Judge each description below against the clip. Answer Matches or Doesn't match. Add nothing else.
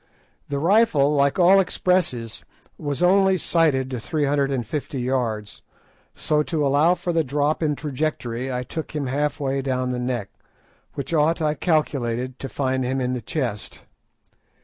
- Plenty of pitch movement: Doesn't match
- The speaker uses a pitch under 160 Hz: Matches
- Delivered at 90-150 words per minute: Doesn't match